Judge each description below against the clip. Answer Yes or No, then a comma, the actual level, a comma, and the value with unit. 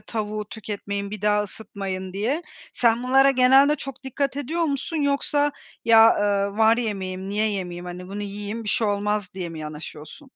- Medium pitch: No, high, 210 Hz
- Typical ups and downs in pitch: Yes, average, 4.6 semitones